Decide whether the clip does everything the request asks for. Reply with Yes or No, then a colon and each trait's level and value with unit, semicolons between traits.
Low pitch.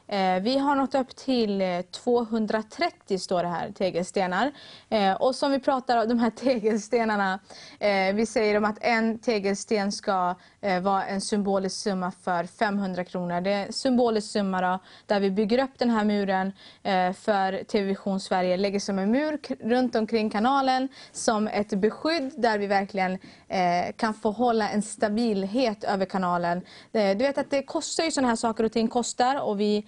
No: high, 215 Hz